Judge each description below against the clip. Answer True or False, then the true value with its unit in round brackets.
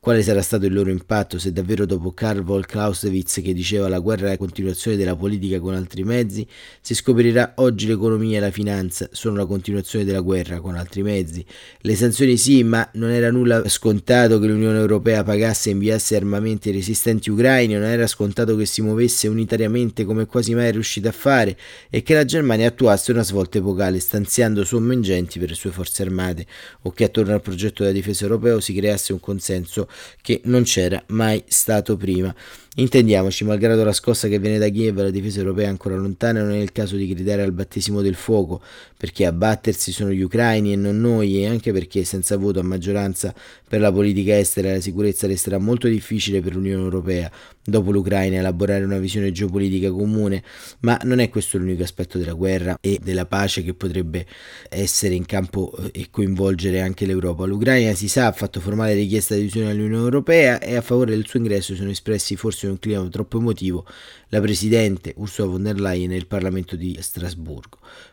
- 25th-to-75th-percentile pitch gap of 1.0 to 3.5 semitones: True (2.6 semitones)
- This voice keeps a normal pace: False (195 wpm)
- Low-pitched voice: True (100 Hz)